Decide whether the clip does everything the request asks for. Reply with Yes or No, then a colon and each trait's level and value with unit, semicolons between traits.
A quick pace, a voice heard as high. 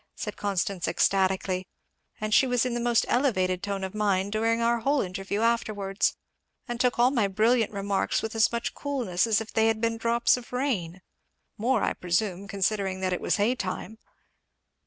No: average, 180 wpm; high, 215 Hz